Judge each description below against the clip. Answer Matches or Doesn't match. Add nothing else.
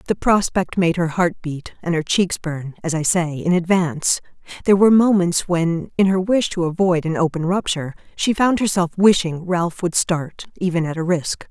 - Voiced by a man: Doesn't match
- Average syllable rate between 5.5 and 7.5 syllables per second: Doesn't match